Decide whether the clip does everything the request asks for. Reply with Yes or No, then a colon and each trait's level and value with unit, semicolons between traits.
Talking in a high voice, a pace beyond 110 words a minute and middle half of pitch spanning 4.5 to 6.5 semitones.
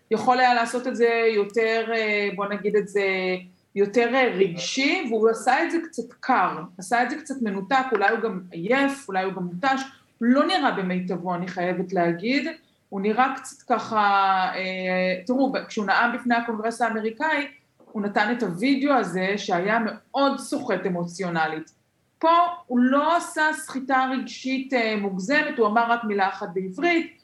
Yes: high, 230 Hz; fast, 150 wpm; average, 5.2 semitones